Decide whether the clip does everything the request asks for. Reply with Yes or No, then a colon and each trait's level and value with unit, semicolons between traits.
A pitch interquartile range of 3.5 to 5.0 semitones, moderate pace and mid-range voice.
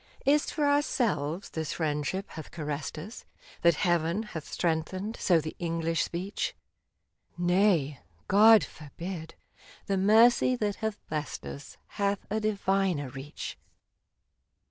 No: average, 4.7 semitones; slow, 130 wpm; medium, 180 Hz